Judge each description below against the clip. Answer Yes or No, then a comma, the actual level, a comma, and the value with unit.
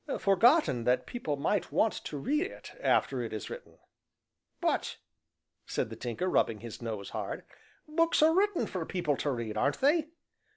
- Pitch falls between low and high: Yes, medium, 160 Hz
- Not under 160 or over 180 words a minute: Yes, average, 165 wpm